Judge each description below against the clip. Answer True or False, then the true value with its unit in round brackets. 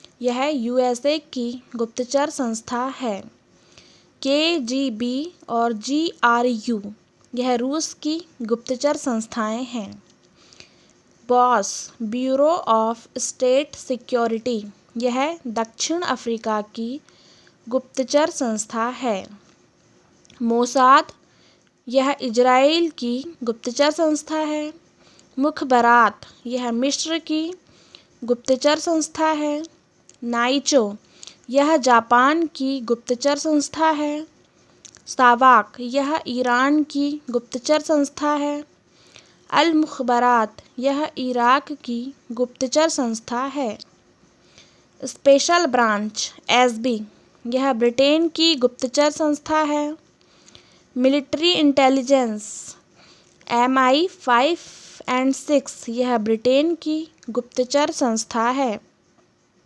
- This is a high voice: True (260 Hz)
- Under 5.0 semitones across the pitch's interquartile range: True (3.6 semitones)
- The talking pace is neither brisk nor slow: False (90 wpm)